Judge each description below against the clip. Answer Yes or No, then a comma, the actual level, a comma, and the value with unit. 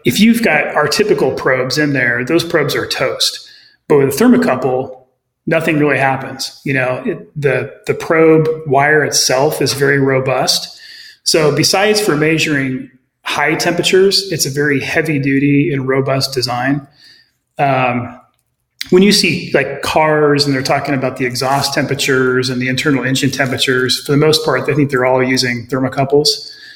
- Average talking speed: Yes, average, 160 wpm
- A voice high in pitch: No, medium, 140 Hz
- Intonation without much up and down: No, average, 3.8 semitones